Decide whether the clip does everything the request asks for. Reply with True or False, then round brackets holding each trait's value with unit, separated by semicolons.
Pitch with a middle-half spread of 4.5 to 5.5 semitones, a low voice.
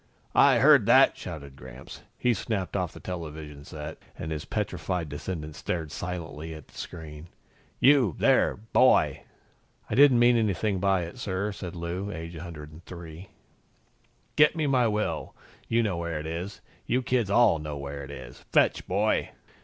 True (5.0 semitones; 85 Hz)